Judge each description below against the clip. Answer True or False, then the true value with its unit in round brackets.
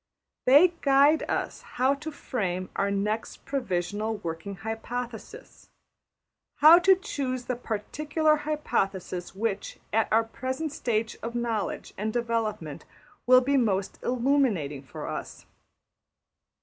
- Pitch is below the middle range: False (235 Hz)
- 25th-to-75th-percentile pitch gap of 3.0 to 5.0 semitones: False (5.4 semitones)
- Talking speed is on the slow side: True (115 wpm)